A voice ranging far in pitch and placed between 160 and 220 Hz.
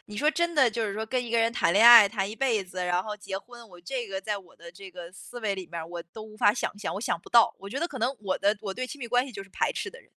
No: average, 3.9 semitones; high, 215 Hz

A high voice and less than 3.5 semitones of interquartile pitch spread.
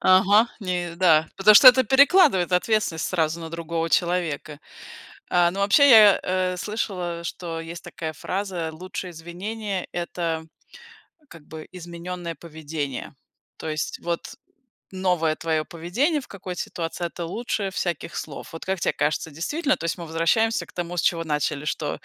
No: medium, 175 Hz; average, 2.9 semitones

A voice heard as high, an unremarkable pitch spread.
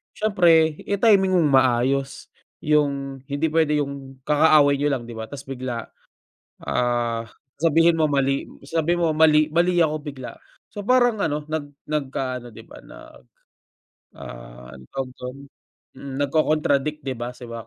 No: medium, 145 Hz; average, 3.5 semitones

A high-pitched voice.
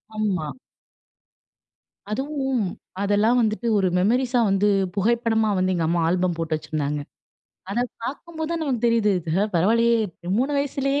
Yes: high, 220 Hz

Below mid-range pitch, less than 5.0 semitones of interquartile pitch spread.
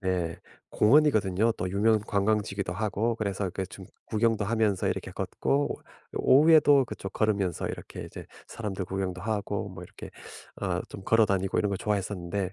Yes: low, 100 Hz; narrow, 2.5 semitones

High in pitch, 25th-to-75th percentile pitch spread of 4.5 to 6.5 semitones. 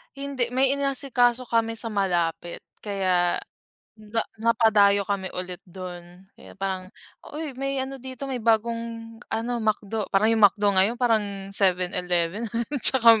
No: high, 220 Hz; average, 3.8 semitones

